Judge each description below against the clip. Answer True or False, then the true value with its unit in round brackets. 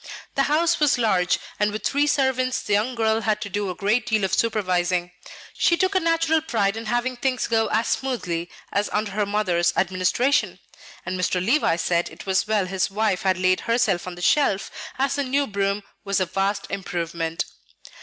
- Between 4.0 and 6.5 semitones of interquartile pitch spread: True (5.4 semitones)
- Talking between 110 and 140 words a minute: False (195 wpm)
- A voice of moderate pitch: False (210 Hz)